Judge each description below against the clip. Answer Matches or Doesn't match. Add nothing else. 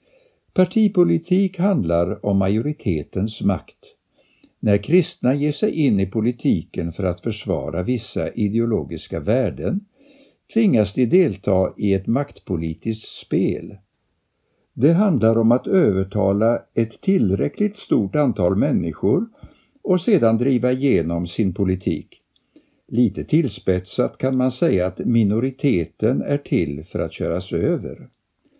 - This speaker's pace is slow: Matches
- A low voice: Matches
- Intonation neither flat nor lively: Doesn't match